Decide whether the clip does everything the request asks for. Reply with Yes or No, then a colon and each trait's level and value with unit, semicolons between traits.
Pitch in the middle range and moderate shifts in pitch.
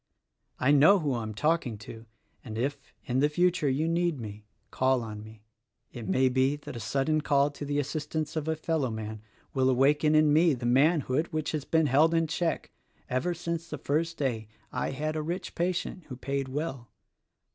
Yes: medium, 145 Hz; average, 3.8 semitones